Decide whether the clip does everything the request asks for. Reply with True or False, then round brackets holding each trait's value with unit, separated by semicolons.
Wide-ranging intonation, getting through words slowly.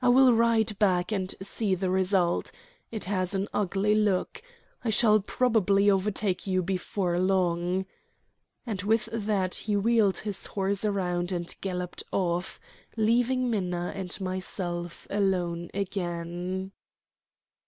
False (2.7 semitones; 125 wpm)